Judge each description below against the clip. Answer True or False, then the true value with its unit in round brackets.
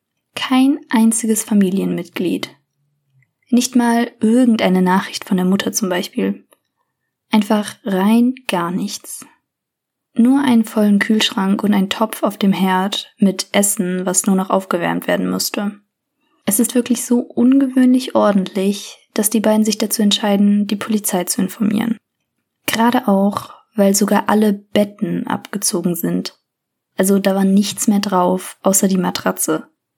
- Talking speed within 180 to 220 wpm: False (135 wpm)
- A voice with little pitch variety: False (3.1 semitones)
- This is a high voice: True (205 Hz)